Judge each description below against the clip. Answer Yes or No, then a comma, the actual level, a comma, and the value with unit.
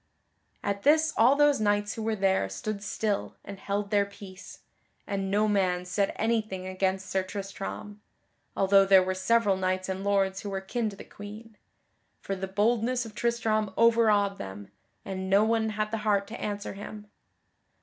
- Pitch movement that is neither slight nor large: No, narrow, 2.1 semitones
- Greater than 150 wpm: Yes, average, 170 wpm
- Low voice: No, high, 200 Hz